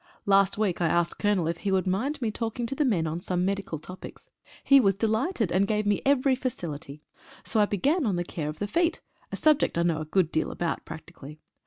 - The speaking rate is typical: No, fast, 230 wpm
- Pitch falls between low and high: No, high, 195 Hz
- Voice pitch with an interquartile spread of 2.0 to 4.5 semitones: No, average, 5.1 semitones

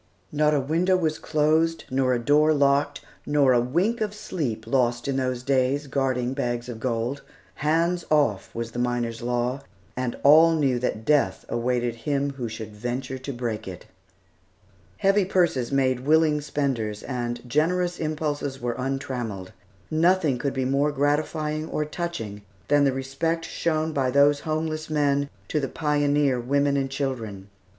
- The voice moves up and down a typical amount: Yes, average, 3.8 semitones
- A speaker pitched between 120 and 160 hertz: Yes, medium, 140 Hz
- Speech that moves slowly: No, average, 155 wpm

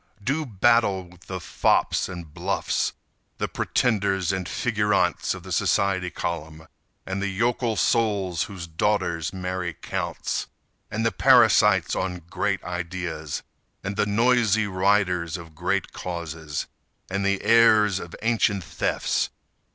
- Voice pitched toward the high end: No, very low, 95 Hz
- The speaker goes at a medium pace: No, slow, 130 wpm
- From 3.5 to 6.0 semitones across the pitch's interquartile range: No, average, 3.1 semitones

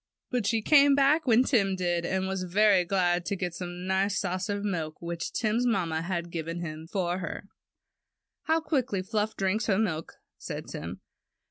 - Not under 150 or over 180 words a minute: Yes, average, 175 wpm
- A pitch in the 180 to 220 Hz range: Yes, high, 190 Hz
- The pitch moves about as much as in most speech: Yes, average, 3.8 semitones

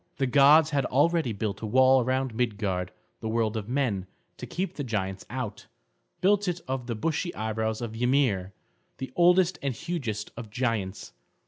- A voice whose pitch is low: Yes, low, 125 Hz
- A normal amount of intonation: Yes, average, 4.6 semitones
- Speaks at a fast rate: No, average, 165 wpm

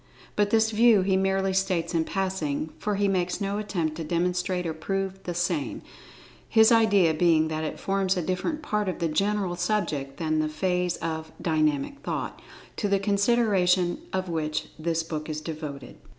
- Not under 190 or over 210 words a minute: No, average, 175 wpm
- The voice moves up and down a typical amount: Yes, average, 3.8 semitones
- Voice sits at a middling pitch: Yes, medium, 180 Hz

